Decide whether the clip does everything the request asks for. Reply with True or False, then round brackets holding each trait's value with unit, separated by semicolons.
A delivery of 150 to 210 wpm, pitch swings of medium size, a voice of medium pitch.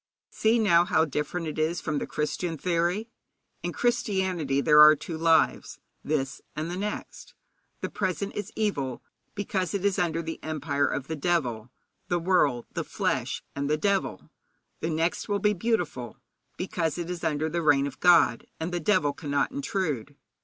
True (170 wpm; 3.9 semitones; 165 Hz)